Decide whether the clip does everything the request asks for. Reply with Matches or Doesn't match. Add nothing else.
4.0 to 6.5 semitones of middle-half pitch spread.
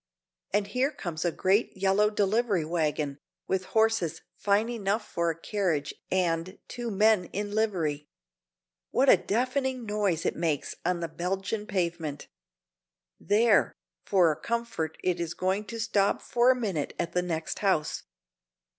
Matches